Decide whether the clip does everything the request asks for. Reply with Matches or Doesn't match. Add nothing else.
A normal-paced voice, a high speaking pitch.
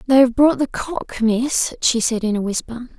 Doesn't match